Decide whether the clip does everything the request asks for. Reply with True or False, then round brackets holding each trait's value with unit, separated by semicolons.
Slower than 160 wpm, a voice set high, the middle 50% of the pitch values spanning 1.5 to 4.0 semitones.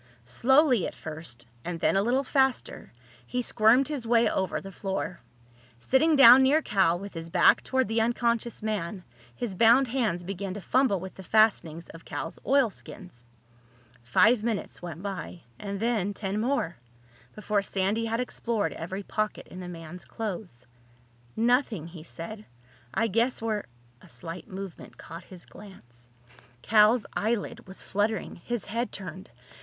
False (150 wpm; 205 Hz; 4.7 semitones)